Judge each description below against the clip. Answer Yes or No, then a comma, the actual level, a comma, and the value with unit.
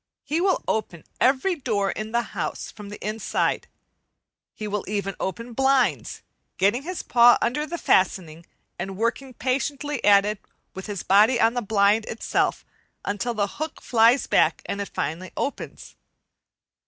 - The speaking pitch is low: No, high, 225 Hz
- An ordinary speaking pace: Yes, average, 155 wpm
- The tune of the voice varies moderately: Yes, average, 4.4 semitones